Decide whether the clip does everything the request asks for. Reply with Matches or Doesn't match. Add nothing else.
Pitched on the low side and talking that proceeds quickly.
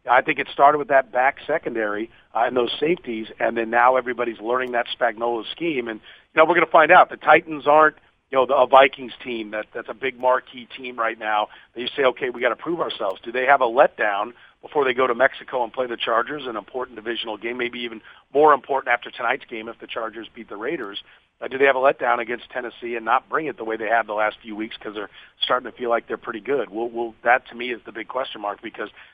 Matches